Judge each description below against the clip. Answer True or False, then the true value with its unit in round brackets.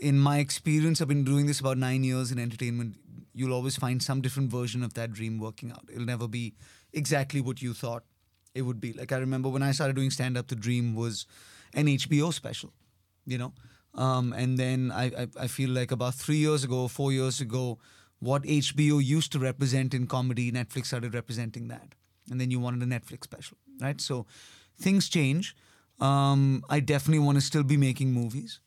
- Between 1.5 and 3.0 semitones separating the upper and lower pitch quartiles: True (2.5 semitones)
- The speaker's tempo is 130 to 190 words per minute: False (200 wpm)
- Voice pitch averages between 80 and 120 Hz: False (130 Hz)